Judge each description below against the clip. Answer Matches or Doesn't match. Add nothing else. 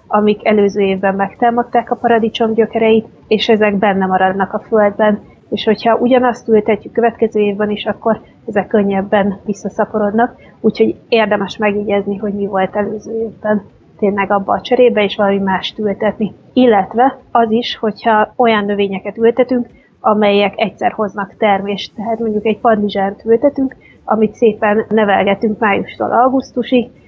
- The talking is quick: Doesn't match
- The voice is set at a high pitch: Matches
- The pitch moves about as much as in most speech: Doesn't match